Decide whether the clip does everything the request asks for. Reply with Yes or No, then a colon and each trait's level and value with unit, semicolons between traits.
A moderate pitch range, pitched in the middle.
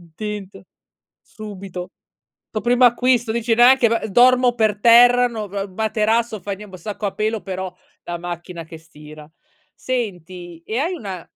No: average, 4.4 semitones; high, 210 Hz